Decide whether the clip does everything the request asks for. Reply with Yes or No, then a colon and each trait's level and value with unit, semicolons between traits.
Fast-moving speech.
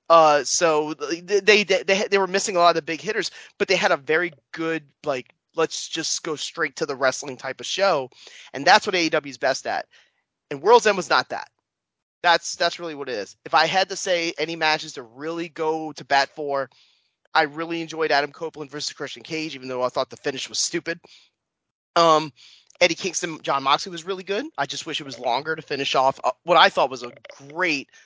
Yes: fast, 215 wpm